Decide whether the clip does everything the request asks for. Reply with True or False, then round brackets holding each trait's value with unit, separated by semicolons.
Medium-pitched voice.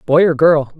True (155 Hz)